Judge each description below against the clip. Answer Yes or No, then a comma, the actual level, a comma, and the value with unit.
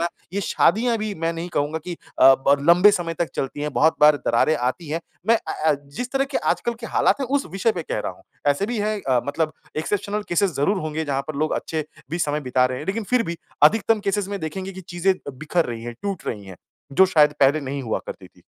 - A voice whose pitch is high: No, medium, 165 Hz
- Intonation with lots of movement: Yes, wide, 5.7 semitones